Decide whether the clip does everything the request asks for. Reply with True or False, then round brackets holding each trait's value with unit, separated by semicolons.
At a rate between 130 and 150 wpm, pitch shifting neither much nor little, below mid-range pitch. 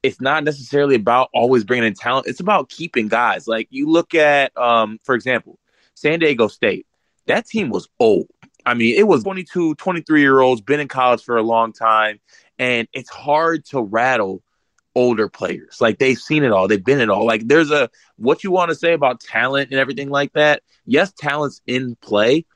False (200 wpm; 4.2 semitones; 130 Hz)